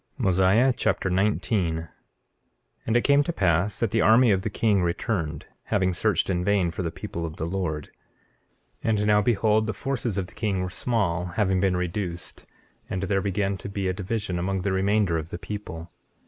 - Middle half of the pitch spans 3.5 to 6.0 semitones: No, average, 3.1 semitones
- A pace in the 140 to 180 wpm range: No, average, 195 wpm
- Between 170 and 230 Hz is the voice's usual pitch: No, very low, 95 Hz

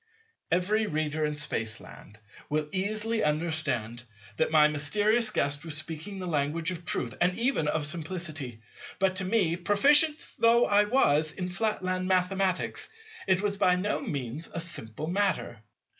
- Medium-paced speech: Yes, average, 145 wpm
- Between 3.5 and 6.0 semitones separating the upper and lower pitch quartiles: Yes, average, 5.0 semitones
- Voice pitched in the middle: Yes, medium, 175 Hz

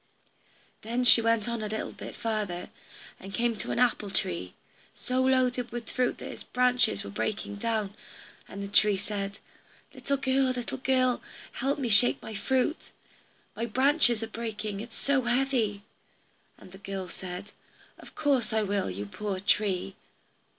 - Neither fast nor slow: Yes, average, 165 wpm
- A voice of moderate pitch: No, high, 225 Hz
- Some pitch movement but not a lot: Yes, average, 3.8 semitones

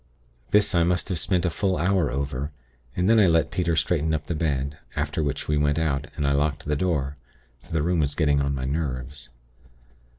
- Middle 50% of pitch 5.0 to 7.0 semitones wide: No, average, 3.4 semitones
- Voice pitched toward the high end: No, very low, 75 Hz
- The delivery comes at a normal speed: No, fast, 210 wpm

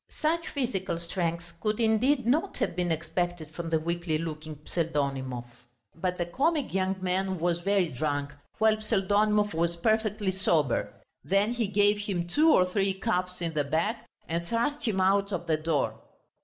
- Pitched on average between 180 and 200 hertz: Yes, medium, 185 Hz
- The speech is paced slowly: No, average, 165 wpm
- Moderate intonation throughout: Yes, average, 4.3 semitones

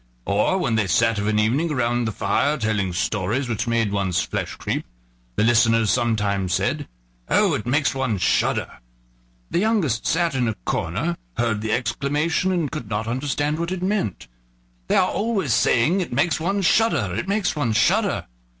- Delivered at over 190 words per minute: No, average, 175 wpm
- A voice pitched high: No, low, 120 Hz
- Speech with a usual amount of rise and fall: No, wide, 7.1 semitones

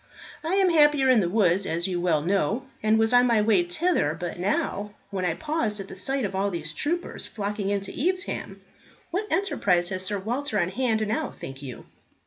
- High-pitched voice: Yes, high, 205 Hz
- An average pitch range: No, wide, 6.6 semitones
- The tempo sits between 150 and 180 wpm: No, fast, 205 wpm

